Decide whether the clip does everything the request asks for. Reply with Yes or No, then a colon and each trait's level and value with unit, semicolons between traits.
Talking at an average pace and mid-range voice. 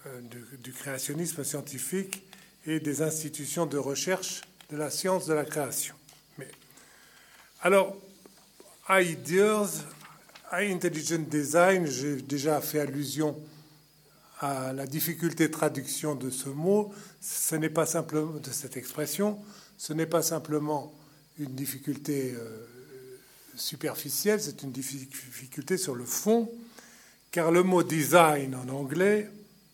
No: slow, 115 wpm; medium, 155 Hz